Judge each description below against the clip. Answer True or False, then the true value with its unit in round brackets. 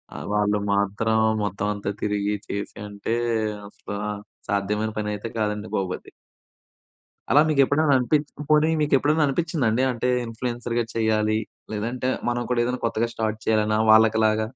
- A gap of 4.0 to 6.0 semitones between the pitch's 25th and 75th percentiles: False (3.1 semitones)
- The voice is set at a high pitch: False (110 Hz)